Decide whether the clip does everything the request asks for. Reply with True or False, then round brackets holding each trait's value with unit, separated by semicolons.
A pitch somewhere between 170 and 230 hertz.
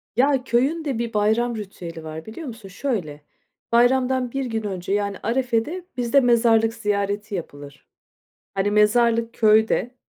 True (225 Hz)